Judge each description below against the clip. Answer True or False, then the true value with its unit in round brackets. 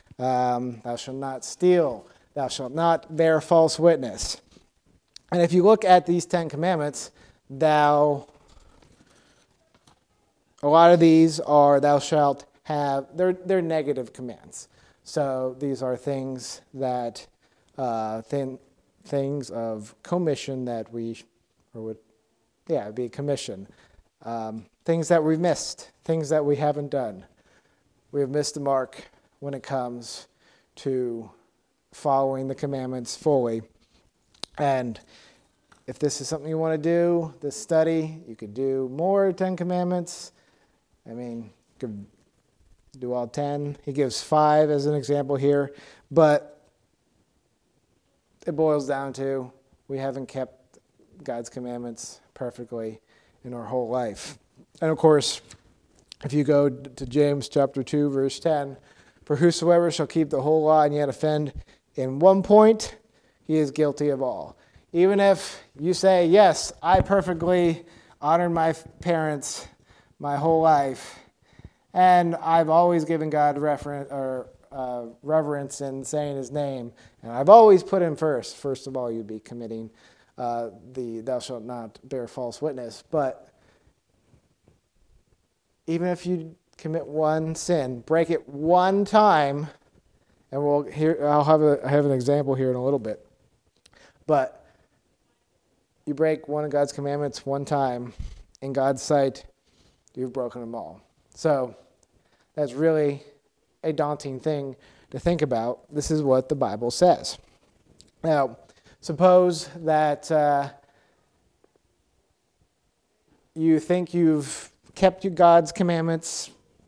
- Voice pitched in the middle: True (145 Hz)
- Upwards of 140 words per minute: False (135 wpm)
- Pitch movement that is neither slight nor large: True (4.0 semitones)